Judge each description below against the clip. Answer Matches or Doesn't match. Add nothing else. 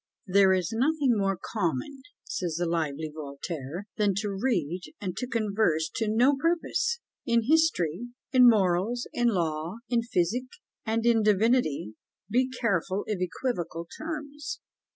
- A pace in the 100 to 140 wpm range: Matches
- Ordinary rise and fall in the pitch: Doesn't match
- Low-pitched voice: Doesn't match